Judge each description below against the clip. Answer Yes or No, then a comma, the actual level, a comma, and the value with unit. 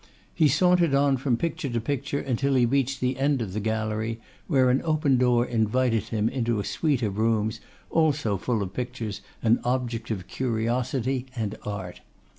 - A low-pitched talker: Yes, low, 120 Hz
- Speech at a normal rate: Yes, average, 175 wpm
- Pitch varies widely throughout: No, average, 3.5 semitones